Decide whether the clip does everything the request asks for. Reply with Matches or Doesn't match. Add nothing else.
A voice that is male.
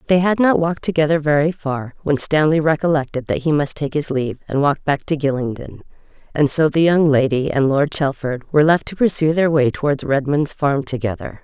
Doesn't match